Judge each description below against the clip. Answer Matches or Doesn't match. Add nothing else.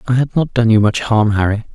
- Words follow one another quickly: Matches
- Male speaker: Matches